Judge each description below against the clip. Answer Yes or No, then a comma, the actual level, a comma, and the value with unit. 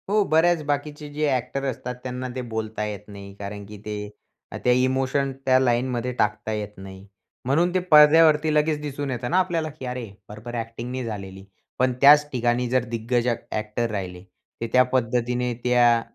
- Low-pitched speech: Yes, low, 125 Hz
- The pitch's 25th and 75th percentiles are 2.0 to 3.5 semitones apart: No, average, 4.5 semitones